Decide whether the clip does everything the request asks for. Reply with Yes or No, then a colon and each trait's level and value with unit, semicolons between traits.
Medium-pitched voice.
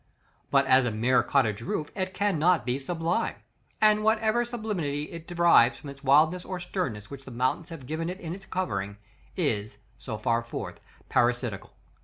Yes: medium, 155 Hz